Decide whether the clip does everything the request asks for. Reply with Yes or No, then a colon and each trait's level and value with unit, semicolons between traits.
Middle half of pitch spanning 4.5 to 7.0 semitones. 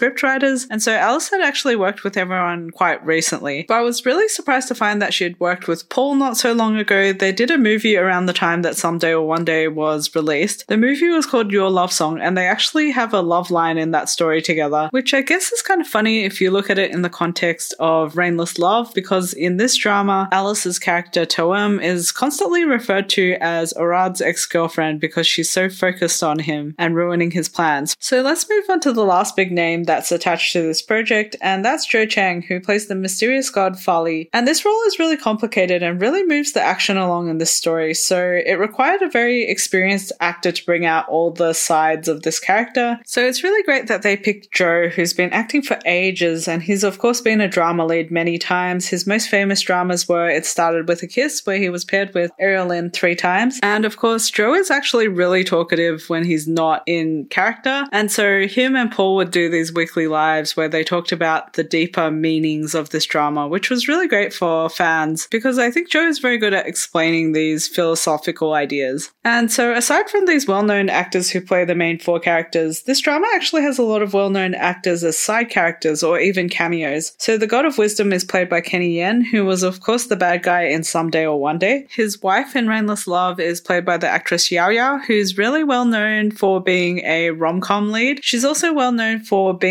Yes: average, 5.1 semitones